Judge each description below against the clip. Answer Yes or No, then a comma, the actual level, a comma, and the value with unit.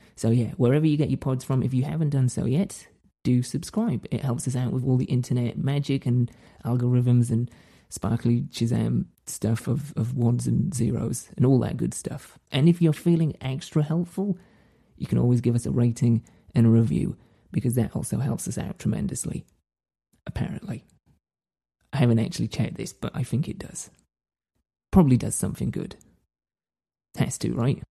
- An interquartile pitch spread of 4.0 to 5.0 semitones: No, average, 2.9 semitones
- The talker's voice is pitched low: Yes, low, 125 Hz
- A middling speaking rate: Yes, average, 175 wpm